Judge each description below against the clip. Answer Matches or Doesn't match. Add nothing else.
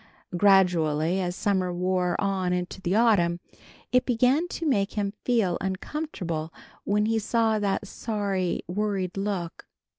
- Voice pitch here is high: Matches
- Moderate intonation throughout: Matches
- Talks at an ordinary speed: Doesn't match